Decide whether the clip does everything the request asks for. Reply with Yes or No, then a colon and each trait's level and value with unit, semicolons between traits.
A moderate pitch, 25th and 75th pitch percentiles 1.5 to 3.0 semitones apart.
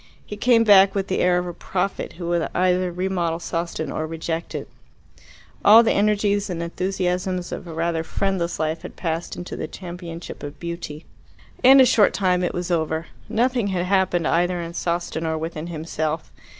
Yes: medium, 175 Hz; narrow, 2.4 semitones